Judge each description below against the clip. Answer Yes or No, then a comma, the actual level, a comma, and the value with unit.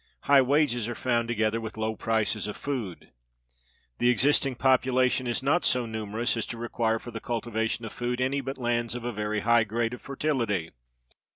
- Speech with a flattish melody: Yes, narrow, 2.3 semitones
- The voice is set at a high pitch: No, low, 120 Hz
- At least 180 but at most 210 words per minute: Yes, average, 185 wpm